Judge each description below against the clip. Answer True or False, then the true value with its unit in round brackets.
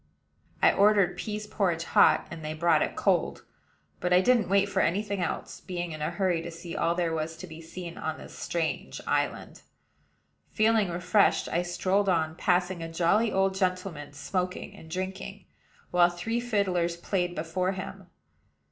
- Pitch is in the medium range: True (180 Hz)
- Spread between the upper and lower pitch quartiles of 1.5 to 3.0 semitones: True (2.6 semitones)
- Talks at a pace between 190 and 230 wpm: False (170 wpm)